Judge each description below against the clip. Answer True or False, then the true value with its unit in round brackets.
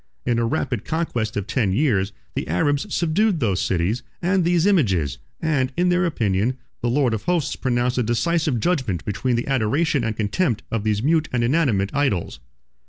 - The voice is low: True (125 Hz)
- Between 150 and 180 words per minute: True (175 wpm)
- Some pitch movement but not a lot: False (6.9 semitones)